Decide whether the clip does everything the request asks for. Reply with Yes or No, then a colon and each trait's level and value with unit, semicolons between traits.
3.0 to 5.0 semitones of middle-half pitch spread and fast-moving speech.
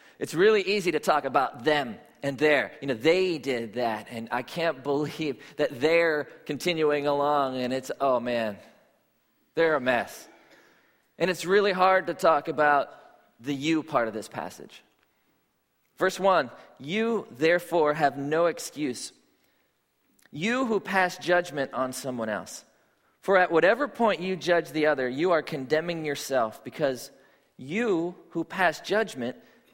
No: average, 4.0 semitones; average, 145 wpm